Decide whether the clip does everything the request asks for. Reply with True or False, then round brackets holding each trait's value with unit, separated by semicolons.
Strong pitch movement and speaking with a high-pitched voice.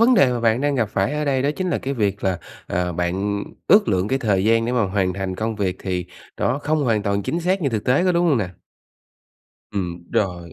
False (6.6 semitones; 110 Hz)